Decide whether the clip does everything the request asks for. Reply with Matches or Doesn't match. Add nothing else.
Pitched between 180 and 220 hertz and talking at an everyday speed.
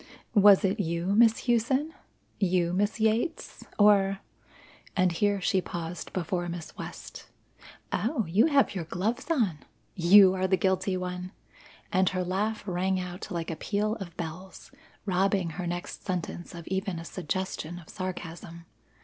Matches